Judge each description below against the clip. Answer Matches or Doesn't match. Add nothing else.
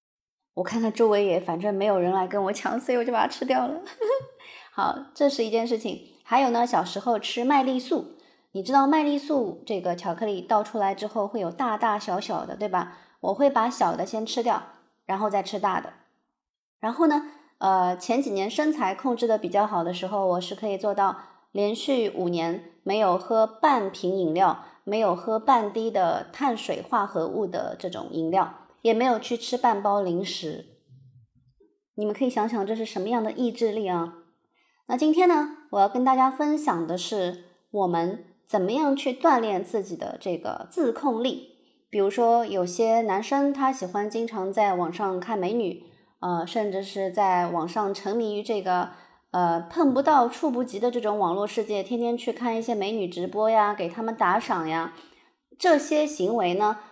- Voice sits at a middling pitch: Doesn't match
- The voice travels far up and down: Doesn't match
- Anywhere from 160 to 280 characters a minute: Matches